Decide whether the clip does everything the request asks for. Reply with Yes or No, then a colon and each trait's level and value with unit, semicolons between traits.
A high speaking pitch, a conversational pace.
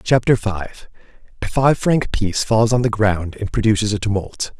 No: low, 110 Hz; average, 170 wpm